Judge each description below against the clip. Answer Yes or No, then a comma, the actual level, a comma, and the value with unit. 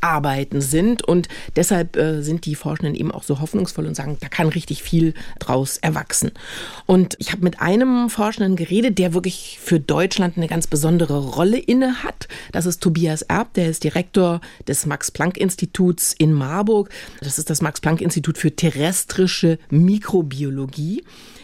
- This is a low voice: No, medium, 170 Hz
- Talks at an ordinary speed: Yes, average, 150 wpm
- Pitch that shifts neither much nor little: Yes, average, 3.2 semitones